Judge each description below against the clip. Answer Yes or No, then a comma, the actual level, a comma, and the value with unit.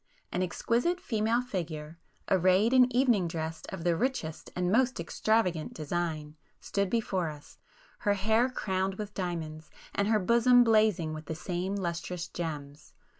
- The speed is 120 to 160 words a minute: Yes, average, 145 wpm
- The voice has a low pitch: No, medium, 185 Hz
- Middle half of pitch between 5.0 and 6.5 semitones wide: Yes, average, 5.3 semitones